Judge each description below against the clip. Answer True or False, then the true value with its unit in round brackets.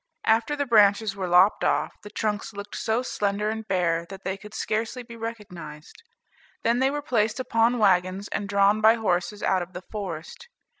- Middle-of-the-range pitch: False (210 Hz)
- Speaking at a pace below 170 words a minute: False (185 wpm)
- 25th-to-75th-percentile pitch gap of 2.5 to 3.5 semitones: True (2.9 semitones)